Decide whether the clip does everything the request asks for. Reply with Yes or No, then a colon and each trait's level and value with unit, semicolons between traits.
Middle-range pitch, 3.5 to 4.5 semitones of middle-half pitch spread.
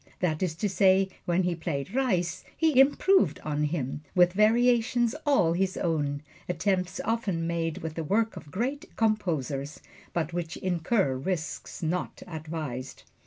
No: medium, 175 Hz; average, 5.2 semitones